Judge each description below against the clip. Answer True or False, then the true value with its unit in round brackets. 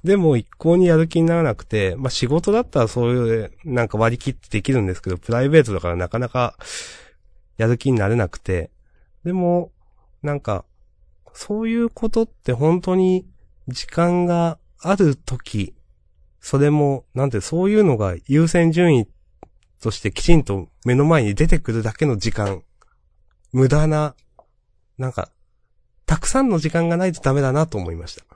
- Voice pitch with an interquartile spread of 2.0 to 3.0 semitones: False (8.0 semitones)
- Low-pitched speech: True (130 Hz)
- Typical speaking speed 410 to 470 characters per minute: False (315 characters per minute)